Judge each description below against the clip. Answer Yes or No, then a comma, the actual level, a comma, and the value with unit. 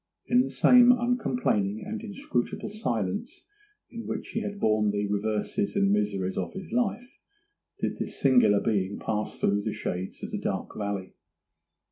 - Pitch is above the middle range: No, low, 120 Hz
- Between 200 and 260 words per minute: No, average, 155 wpm